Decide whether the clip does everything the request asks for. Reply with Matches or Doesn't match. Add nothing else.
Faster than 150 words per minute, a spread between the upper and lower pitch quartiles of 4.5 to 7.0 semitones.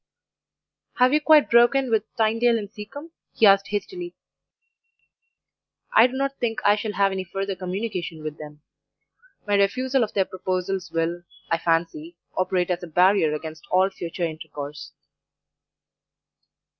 Doesn't match